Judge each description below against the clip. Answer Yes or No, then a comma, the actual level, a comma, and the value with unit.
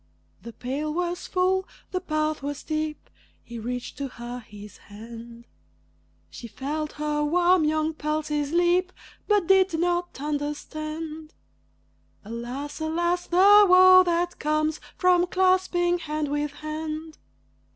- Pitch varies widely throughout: No, average, 3.3 semitones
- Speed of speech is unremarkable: No, slow, 120 wpm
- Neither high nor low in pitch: No, very high, 310 Hz